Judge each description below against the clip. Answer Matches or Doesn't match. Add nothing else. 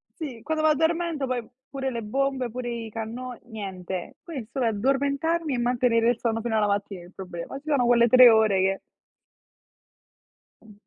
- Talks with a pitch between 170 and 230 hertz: Doesn't match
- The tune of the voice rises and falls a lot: Doesn't match